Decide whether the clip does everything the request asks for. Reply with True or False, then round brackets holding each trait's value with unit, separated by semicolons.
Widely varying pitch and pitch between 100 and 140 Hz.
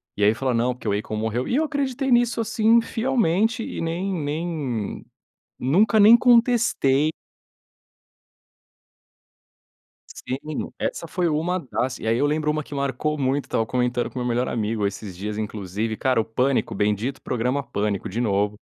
True (8.2 semitones; 135 Hz)